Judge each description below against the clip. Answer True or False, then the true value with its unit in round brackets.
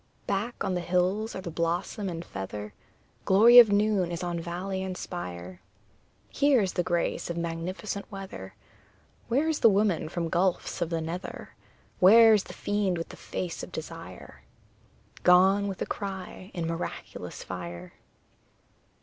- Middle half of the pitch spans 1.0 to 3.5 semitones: True (3.1 semitones)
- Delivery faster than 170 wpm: False (155 wpm)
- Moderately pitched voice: True (180 Hz)